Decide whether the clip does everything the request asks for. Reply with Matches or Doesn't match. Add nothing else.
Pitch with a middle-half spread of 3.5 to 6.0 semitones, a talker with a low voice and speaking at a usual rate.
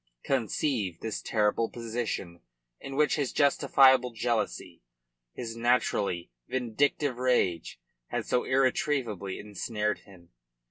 Doesn't match